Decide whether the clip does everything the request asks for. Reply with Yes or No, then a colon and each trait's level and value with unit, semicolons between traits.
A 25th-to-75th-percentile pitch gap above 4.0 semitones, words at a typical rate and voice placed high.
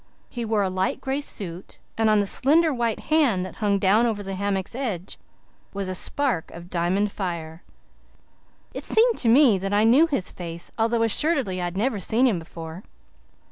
Yes: average, 4.6 semitones; average, 185 wpm; high, 205 Hz